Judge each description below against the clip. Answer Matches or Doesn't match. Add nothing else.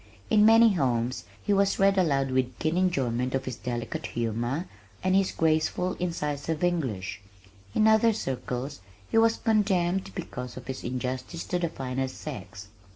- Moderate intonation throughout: Doesn't match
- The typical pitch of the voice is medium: Matches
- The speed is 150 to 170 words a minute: Matches